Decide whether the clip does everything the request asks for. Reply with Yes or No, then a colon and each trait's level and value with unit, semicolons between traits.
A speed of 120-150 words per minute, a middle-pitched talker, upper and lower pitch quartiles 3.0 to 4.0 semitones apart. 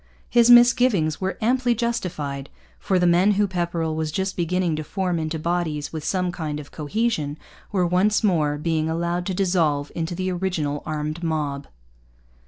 No: average, 165 wpm; medium, 170 Hz; average, 3.5 semitones